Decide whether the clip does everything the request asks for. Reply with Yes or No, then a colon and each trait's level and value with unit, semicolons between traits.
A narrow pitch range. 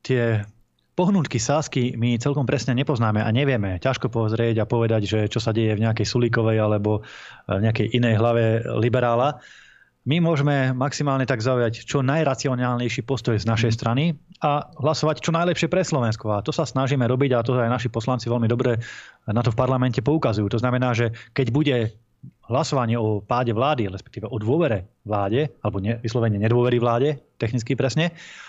No: average, 3.2 semitones